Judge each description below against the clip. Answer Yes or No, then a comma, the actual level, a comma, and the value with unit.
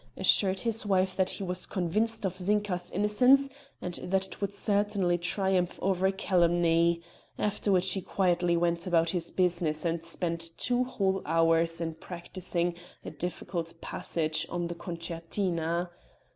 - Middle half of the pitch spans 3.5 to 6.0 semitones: No, narrow, 2.4 semitones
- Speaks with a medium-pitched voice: Yes, medium, 180 Hz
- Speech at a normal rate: Yes, average, 145 wpm